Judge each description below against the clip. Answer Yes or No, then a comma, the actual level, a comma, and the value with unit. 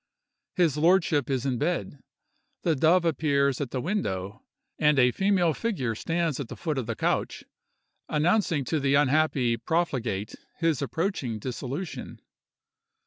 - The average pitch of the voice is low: No, medium, 150 Hz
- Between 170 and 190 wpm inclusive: No, average, 140 wpm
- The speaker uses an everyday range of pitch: Yes, average, 4.7 semitones